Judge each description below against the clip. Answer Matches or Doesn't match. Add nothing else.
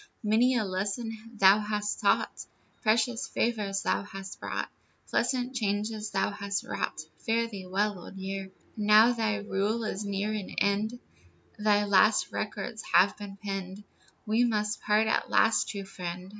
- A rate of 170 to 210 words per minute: Doesn't match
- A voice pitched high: Matches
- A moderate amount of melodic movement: Doesn't match